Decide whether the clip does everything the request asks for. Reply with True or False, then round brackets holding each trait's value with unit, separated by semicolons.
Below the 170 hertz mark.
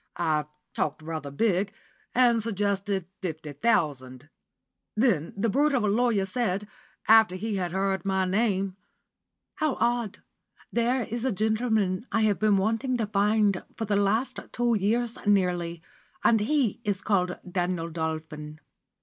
False (200 Hz)